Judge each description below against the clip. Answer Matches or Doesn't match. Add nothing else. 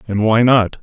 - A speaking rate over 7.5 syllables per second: Doesn't match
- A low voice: Matches